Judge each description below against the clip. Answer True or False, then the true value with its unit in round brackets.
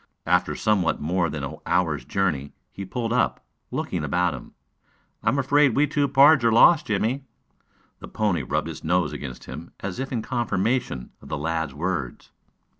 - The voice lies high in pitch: False (95 Hz)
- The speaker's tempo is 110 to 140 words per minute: False (175 wpm)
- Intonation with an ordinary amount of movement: False (7.9 semitones)